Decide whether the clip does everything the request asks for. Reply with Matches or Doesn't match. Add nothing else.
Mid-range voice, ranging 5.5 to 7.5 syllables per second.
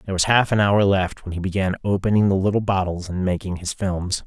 Doesn't match